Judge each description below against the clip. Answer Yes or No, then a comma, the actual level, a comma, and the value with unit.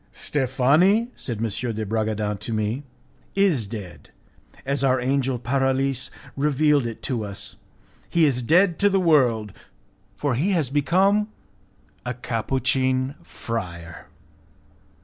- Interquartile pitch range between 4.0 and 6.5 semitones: Yes, average, 4.6 semitones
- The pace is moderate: No, slow, 120 wpm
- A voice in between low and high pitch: No, low, 130 Hz